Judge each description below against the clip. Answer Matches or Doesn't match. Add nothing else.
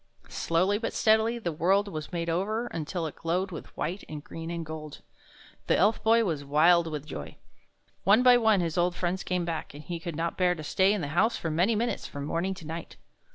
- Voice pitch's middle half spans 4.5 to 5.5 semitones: Doesn't match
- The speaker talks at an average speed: Doesn't match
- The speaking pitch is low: Doesn't match